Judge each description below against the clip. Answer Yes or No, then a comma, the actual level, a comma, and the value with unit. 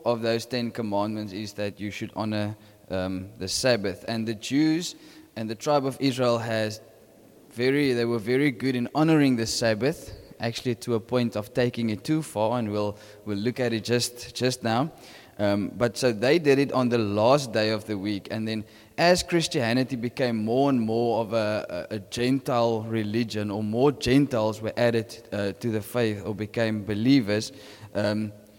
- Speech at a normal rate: Yes, average, 185 wpm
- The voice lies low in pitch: Yes, low, 115 Hz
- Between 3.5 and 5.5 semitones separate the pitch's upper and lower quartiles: No, average, 3.0 semitones